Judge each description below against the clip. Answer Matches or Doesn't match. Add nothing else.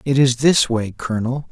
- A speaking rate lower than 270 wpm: Matches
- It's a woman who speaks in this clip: Doesn't match